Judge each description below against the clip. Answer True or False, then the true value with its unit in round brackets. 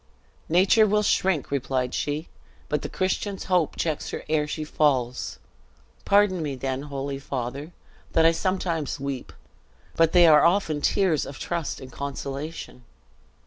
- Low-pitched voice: False (155 Hz)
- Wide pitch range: False (4.3 semitones)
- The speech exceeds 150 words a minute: False (145 wpm)